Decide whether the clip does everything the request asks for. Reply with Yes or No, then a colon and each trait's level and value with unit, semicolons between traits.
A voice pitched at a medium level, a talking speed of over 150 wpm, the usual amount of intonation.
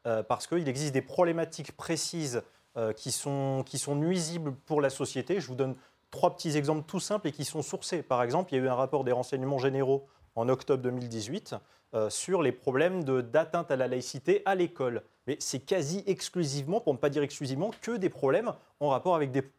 Yes: medium, 145 Hz; average, 200 wpm; average, 4.5 semitones